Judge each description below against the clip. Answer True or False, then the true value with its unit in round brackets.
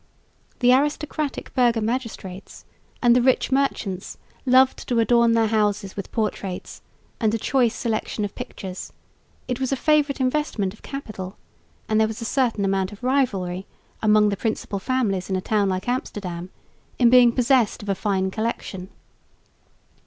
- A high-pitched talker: True (225 Hz)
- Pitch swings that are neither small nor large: True (4.3 semitones)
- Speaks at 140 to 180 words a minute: True (155 wpm)